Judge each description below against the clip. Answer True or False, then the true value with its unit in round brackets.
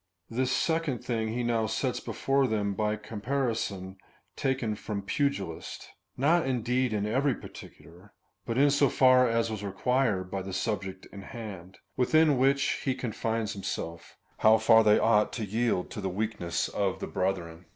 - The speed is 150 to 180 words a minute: True (170 wpm)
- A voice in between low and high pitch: False (110 Hz)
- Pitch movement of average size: True (4.3 semitones)